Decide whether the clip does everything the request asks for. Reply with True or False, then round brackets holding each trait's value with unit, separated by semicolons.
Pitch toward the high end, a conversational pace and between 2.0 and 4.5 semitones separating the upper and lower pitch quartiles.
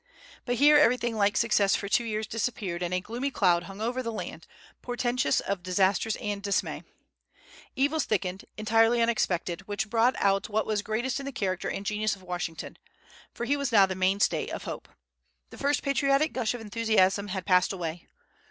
True (215 Hz; 180 wpm; 3.8 semitones)